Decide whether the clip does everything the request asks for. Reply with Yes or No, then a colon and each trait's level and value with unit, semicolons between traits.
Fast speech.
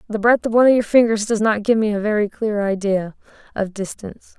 Yes: fast, 235 wpm